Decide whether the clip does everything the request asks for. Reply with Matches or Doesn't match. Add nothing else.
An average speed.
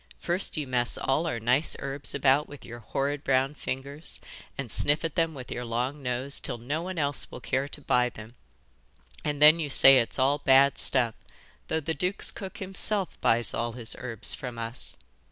Matches